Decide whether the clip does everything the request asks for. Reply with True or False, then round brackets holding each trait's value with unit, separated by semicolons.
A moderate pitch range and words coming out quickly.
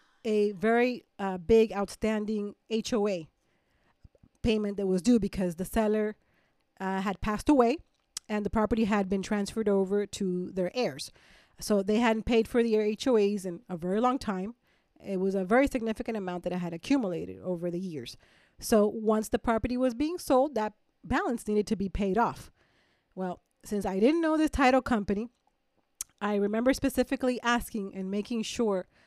False (3.3 semitones; 165 wpm)